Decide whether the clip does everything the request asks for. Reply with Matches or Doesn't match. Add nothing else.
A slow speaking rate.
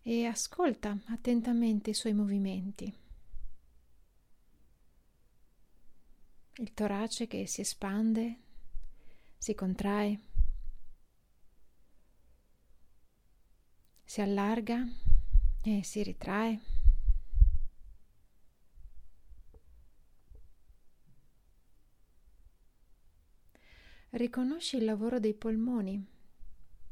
Matches